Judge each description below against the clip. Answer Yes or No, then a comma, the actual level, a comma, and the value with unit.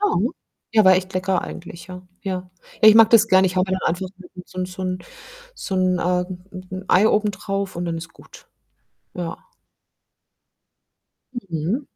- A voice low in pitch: No, medium, 185 Hz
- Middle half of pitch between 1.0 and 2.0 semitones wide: Yes, narrow, 1.4 semitones